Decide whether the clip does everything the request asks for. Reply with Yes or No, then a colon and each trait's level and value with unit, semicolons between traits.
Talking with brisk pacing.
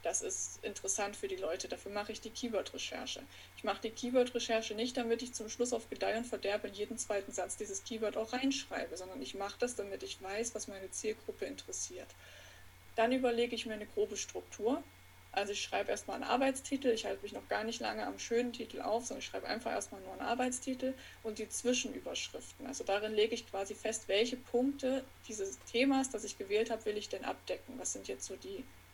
Yes: fast, 210 wpm